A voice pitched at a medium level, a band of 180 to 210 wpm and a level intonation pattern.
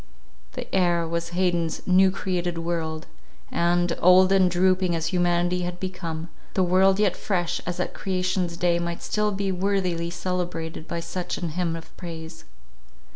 No: medium, 175 Hz; average, 155 wpm; narrow, 1.6 semitones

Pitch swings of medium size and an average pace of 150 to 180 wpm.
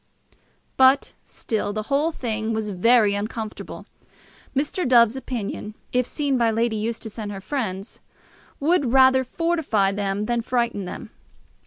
No: average, 3.7 semitones; slow, 135 wpm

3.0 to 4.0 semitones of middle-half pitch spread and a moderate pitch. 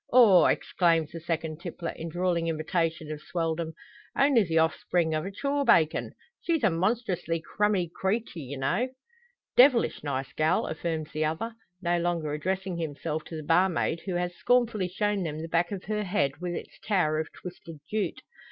Yes: average, 3.3 semitones; medium, 170 Hz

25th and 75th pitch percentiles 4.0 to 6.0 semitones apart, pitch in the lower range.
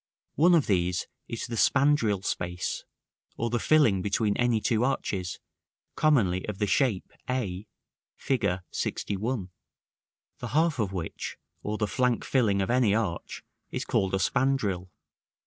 Yes: average, 5.1 semitones; low, 110 Hz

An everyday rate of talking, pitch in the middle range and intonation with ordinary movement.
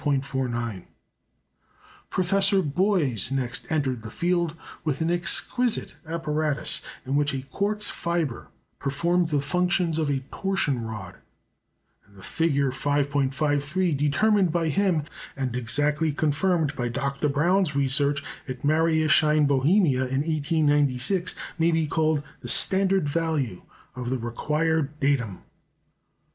No: slow, 115 wpm; medium, 150 Hz; average, 3.5 semitones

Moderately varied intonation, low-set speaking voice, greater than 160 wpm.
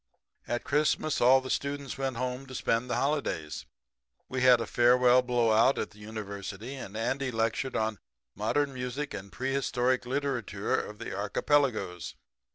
No: average, 3.5 semitones; low, 125 Hz; average, 150 wpm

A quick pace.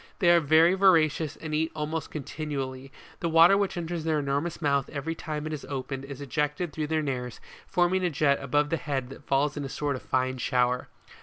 Yes: fast, 210 wpm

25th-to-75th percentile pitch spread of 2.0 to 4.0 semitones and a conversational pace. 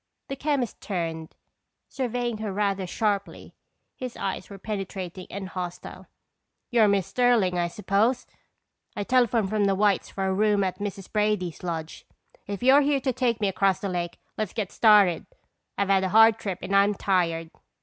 Yes: average, 2.9 semitones; average, 170 wpm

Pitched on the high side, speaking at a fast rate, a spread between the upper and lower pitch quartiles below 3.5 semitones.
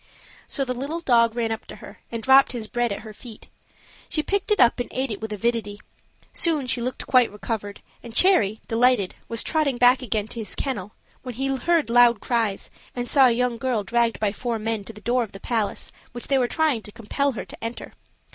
Yes: high, 235 Hz; fast, 220 wpm; average, 2.9 semitones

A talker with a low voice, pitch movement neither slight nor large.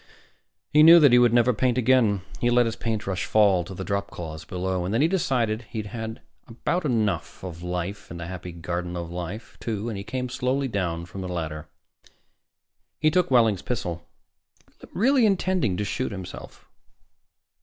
No: low, 105 Hz; wide, 5.7 semitones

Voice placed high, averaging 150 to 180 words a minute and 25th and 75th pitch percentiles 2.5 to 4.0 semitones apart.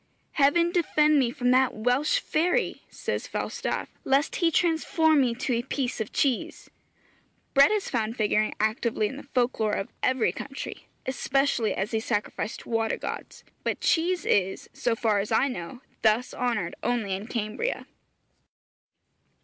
No: high, 245 Hz; average, 155 wpm; average, 4.5 semitones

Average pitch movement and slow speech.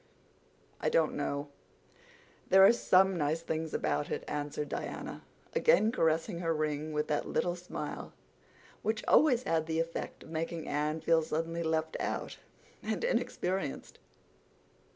Yes: average, 3.6 semitones; slow, 130 wpm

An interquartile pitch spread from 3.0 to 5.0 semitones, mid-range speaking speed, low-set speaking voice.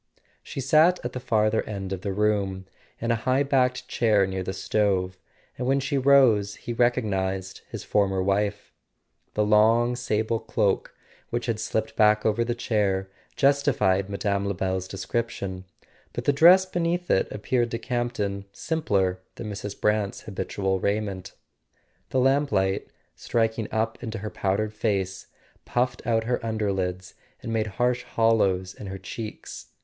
Yes: average, 3.7 semitones; average, 150 wpm; low, 105 Hz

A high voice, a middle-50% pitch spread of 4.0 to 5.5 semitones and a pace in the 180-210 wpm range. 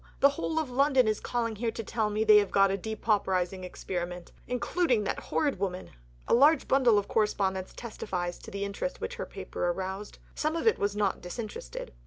Yes: high, 210 Hz; average, 4.7 semitones; average, 195 wpm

